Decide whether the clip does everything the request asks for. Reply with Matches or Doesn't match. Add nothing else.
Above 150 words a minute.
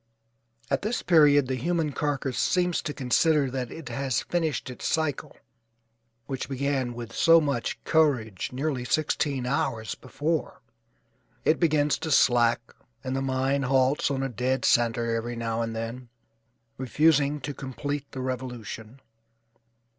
Doesn't match